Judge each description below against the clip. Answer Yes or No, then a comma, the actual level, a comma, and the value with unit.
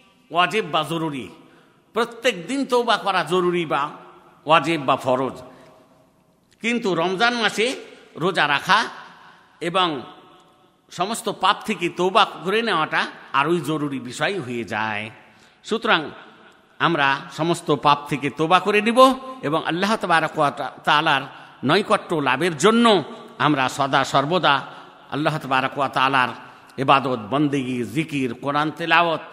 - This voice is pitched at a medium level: Yes, medium, 160 Hz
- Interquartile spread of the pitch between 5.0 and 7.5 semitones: Yes, wide, 5.4 semitones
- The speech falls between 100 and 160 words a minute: Yes, average, 110 wpm